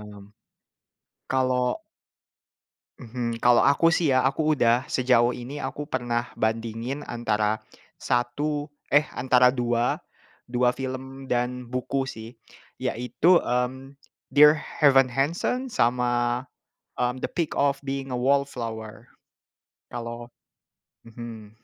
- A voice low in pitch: Yes, low, 125 Hz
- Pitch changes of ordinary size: No, narrow, 2.3 semitones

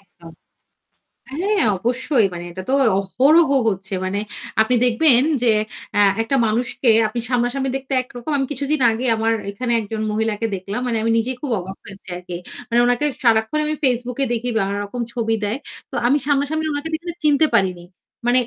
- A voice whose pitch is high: Yes, high, 240 Hz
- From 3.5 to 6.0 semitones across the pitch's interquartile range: Yes, average, 4.1 semitones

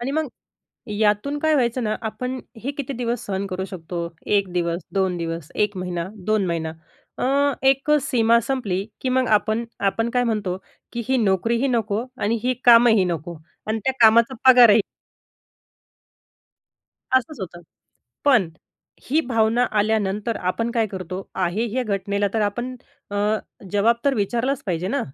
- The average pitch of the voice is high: Yes, high, 220 Hz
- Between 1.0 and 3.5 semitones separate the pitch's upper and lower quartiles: No, average, 4.3 semitones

